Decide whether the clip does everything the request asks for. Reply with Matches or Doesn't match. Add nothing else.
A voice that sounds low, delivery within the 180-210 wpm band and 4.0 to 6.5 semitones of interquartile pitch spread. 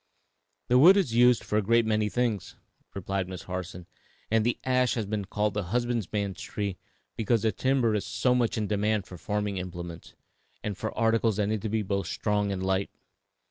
Doesn't match